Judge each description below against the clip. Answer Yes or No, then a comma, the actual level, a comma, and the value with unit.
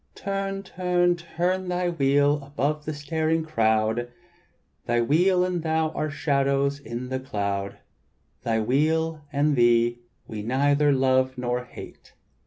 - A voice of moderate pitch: Yes, medium, 145 Hz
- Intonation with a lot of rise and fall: No, average, 4.7 semitones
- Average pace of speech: No, slow, 125 wpm